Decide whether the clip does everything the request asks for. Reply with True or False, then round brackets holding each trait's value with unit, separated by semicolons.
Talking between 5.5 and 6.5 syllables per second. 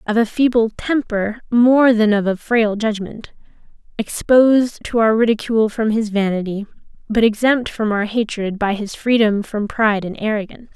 False (4.9 syllables/s)